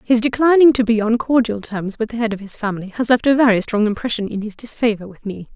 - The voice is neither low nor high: No, high, 225 Hz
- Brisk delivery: Yes, fast, 260 wpm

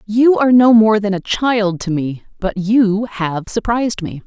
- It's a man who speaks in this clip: No, female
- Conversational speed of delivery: Yes, average, 195 wpm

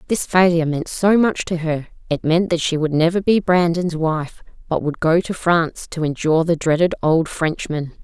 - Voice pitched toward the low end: No, medium, 165 Hz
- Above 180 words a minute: Yes, average, 200 wpm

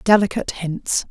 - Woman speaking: Yes, female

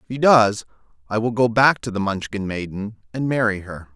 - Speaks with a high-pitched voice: No, low, 110 Hz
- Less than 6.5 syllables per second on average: Yes, 5.3 syllables/s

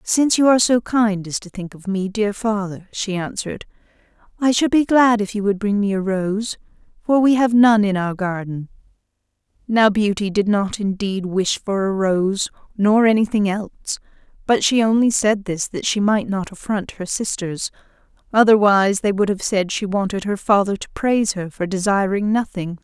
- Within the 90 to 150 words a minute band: No, average, 185 wpm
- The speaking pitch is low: No, high, 205 Hz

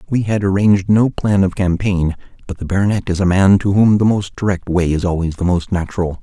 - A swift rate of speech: Yes, fast, 230 wpm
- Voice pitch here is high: No, very low, 95 Hz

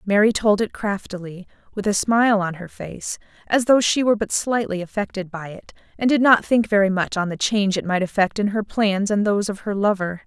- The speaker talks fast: Yes, fast, 230 wpm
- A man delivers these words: No, female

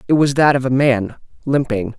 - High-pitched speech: No, low, 130 Hz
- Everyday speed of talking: No, fast, 210 wpm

